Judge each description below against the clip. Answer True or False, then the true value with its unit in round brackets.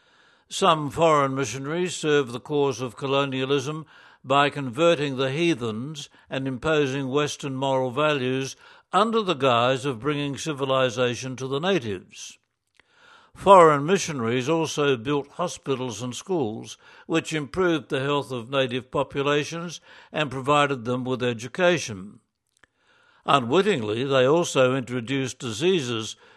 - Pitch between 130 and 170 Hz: True (140 Hz)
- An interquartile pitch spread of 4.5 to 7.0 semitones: False (3.2 semitones)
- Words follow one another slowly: True (115 wpm)